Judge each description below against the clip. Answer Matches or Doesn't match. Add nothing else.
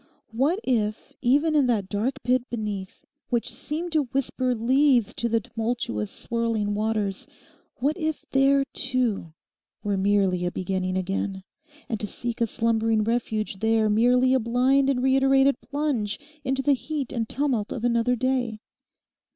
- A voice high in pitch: Matches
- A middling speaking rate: Matches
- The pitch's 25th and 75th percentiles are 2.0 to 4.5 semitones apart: Matches